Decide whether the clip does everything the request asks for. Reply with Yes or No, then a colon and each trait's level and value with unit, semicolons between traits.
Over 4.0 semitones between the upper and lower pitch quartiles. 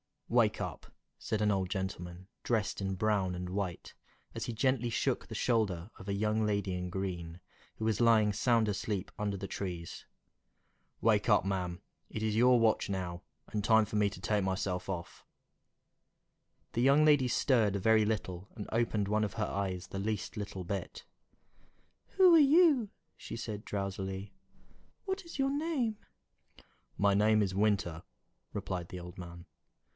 No: average, 2.9 semitones